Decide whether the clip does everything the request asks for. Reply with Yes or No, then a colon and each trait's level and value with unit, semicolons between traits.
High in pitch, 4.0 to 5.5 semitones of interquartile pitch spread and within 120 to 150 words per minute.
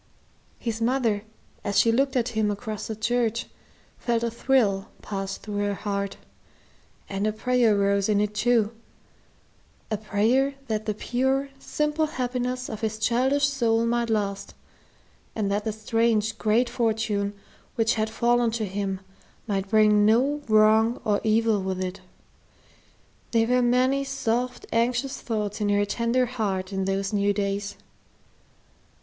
No: high, 220 Hz; average, 2.9 semitones; average, 145 wpm